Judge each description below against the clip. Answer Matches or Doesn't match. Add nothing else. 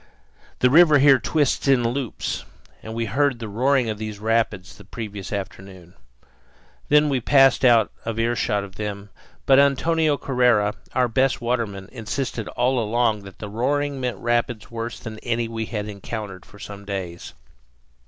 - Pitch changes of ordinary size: Matches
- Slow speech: Doesn't match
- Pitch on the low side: Matches